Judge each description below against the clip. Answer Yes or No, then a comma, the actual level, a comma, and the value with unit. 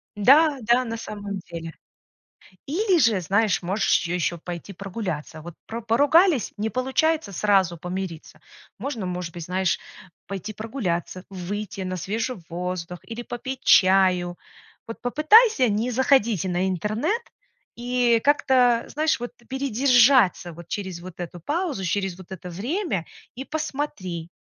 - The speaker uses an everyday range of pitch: No, wide, 6.0 semitones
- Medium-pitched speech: No, high, 210 Hz